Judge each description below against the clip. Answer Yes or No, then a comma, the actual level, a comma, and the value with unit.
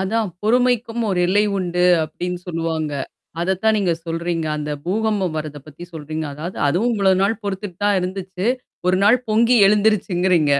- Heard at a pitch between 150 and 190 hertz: Yes, medium, 185 Hz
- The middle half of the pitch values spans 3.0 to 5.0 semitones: Yes, average, 4.2 semitones